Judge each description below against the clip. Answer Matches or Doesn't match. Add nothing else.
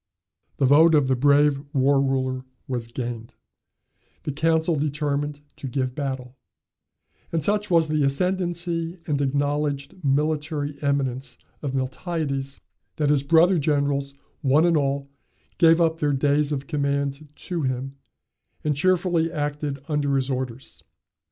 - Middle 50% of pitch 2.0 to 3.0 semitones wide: Matches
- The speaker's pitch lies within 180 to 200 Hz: Doesn't match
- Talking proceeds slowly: Matches